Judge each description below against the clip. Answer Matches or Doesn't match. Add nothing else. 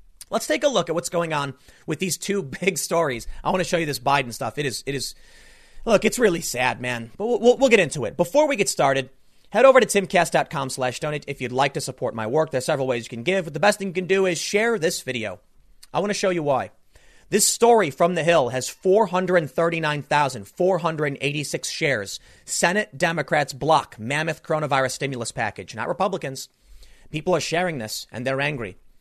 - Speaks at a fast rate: Matches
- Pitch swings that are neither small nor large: Doesn't match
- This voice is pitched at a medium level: Matches